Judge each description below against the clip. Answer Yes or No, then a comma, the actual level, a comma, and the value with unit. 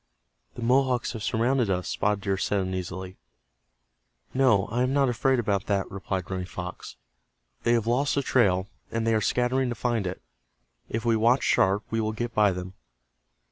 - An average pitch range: Yes, average, 4.1 semitones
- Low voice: Yes, low, 110 Hz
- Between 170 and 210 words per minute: Yes, average, 180 wpm